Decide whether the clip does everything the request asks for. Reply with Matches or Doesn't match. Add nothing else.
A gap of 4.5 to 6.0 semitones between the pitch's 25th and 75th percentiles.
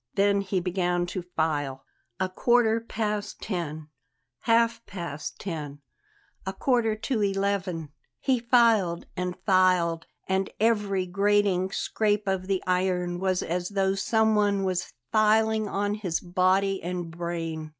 Doesn't match